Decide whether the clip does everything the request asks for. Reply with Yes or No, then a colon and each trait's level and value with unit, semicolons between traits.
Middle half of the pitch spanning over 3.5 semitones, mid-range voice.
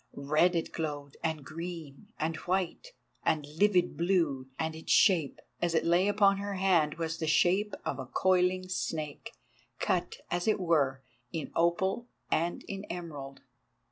No: average, 3.2 semitones; medium, 170 Hz